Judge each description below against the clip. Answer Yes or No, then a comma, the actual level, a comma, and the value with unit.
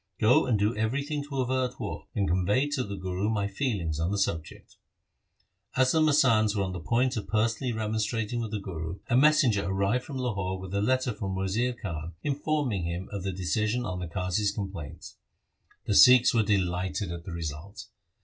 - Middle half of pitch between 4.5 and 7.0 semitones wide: Yes, average, 4.9 semitones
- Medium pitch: No, low, 105 Hz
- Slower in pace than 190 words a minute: No, average, 195 wpm